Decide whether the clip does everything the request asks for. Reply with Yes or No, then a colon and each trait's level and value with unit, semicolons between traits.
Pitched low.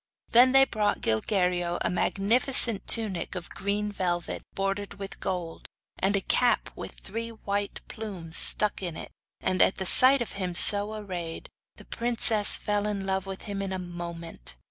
No: high, 195 Hz